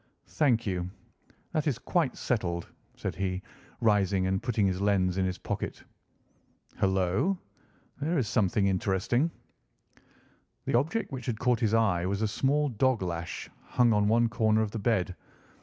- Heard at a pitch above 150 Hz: No, low, 105 Hz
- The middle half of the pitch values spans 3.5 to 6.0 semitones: Yes, average, 4.6 semitones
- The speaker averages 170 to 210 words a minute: No, average, 155 wpm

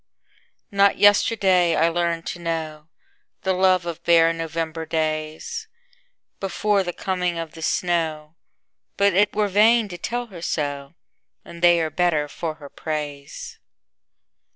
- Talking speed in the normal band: No, slow, 120 wpm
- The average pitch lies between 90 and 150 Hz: No, medium, 170 Hz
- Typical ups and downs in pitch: Yes, average, 3.5 semitones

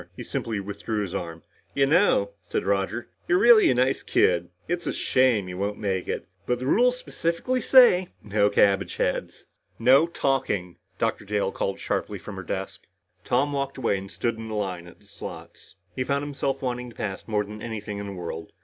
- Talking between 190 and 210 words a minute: Yes, average, 195 wpm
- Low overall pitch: Yes, low, 110 Hz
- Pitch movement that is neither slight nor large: No, wide, 5.7 semitones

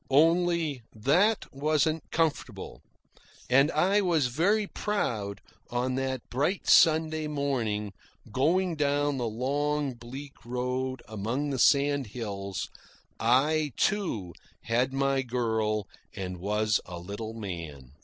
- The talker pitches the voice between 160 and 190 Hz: No, low, 130 Hz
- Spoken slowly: Yes, slow, 110 wpm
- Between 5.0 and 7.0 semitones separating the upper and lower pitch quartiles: Yes, wide, 5.6 semitones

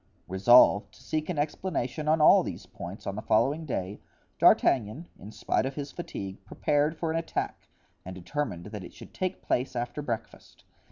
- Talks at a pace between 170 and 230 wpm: Yes, average, 175 wpm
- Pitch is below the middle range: Yes, low, 125 Hz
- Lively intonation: Yes, wide, 7.1 semitones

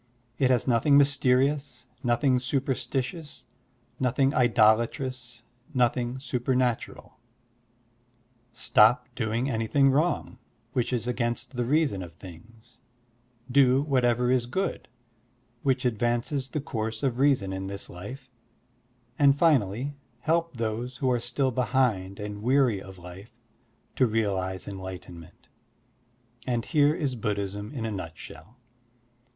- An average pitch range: Yes, average, 3.6 semitones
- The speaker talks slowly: Yes, slow, 115 wpm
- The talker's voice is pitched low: Yes, low, 120 Hz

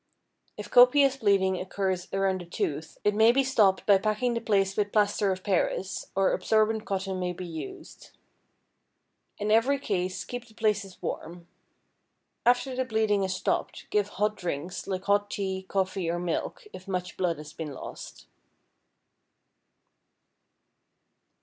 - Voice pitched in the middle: No, high, 195 Hz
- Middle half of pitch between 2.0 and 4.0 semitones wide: Yes, average, 2.8 semitones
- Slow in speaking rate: No, average, 145 wpm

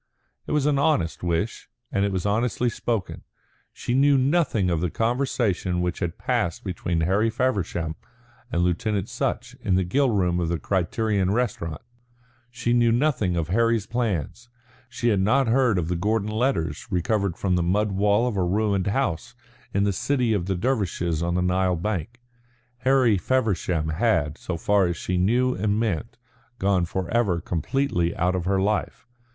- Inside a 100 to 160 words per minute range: No, average, 170 wpm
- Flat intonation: No, average, 5.0 semitones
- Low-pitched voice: Yes, low, 100 Hz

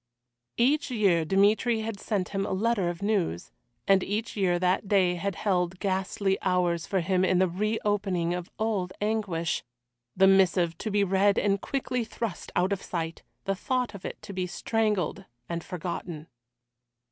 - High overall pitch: Yes, high, 195 Hz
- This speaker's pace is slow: No, average, 165 wpm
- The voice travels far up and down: No, average, 2.7 semitones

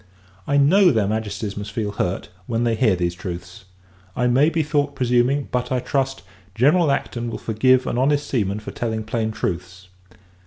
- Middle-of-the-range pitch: No, low, 120 Hz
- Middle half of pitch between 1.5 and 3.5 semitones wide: No, average, 4.6 semitones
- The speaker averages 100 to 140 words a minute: No, average, 180 wpm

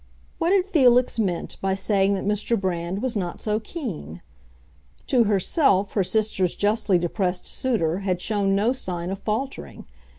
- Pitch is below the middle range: No, high, 200 Hz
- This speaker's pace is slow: No, average, 155 wpm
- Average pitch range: Yes, average, 3.8 semitones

